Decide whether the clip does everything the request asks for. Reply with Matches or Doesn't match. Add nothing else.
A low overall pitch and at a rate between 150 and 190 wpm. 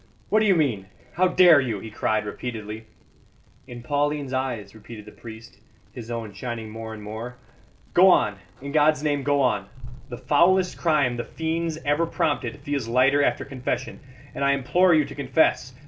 Matches